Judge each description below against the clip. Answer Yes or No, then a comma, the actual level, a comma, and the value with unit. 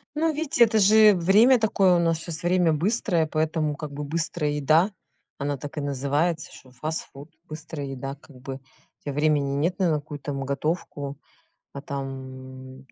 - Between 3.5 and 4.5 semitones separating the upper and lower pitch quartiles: Yes, average, 3.8 semitones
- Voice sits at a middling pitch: Yes, medium, 155 Hz